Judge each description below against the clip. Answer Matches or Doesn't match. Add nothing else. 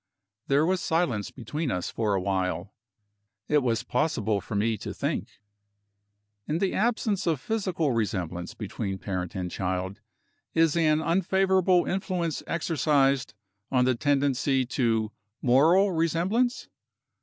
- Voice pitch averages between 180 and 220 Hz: Doesn't match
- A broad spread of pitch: Matches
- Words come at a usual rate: Doesn't match